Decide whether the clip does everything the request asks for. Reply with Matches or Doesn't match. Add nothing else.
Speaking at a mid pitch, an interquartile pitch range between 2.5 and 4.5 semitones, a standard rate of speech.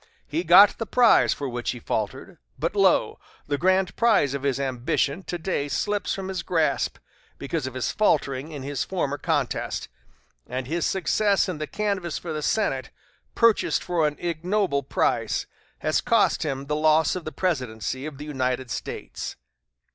Doesn't match